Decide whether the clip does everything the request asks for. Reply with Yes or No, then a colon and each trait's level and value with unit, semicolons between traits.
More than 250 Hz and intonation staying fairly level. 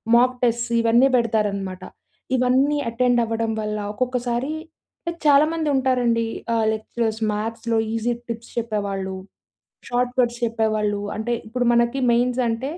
No: high, 235 Hz; narrow, 2.1 semitones